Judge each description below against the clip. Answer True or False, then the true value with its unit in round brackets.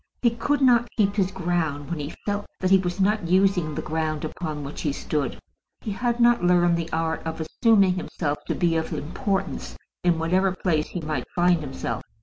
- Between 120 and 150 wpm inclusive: False (195 wpm)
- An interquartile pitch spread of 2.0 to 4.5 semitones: True (3.7 semitones)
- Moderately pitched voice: True (175 Hz)